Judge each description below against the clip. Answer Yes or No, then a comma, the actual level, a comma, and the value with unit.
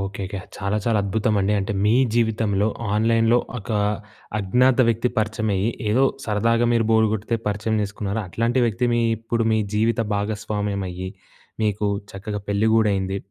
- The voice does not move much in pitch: Yes, narrow, 2.0 semitones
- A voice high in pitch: No, low, 105 Hz